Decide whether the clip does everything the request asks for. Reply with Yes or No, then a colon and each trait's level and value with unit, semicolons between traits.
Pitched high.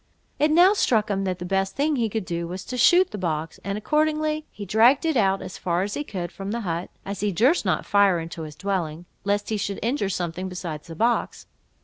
Yes: high, 200 Hz